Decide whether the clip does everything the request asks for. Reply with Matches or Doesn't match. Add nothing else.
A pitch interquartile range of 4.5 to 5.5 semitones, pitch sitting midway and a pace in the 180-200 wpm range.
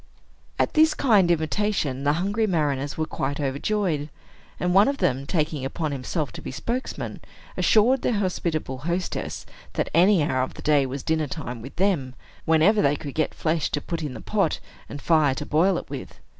Matches